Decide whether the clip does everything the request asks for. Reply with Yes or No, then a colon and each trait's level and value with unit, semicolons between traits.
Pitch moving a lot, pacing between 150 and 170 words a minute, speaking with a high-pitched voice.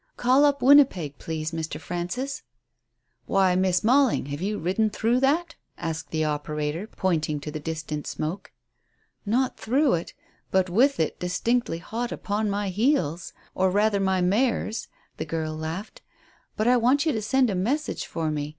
Yes: wide, 7.1 semitones; average, 160 wpm; high, 195 Hz